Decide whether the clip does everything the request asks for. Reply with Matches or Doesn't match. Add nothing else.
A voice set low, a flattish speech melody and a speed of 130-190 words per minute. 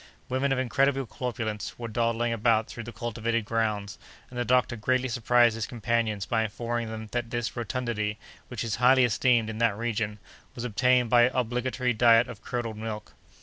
Matches